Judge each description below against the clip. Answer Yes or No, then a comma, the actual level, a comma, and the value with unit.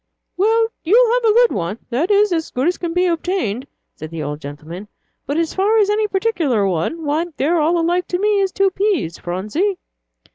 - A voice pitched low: No, very high, 345 Hz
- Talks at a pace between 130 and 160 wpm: No, average, 195 wpm